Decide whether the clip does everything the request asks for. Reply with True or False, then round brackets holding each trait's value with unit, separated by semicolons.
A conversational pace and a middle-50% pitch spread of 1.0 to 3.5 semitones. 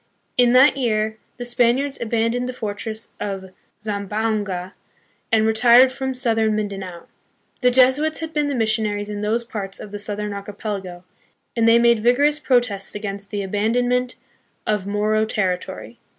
True (155 wpm; 3.1 semitones)